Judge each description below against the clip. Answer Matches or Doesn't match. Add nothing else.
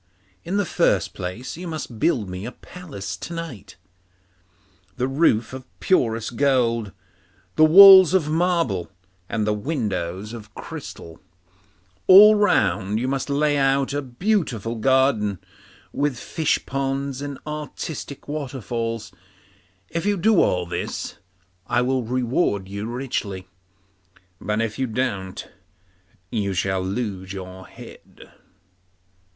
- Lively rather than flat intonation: Matches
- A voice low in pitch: Matches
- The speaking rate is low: Matches